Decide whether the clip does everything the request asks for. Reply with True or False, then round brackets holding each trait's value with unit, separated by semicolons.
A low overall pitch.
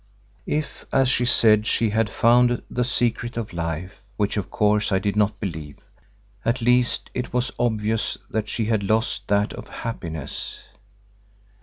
True (110 Hz)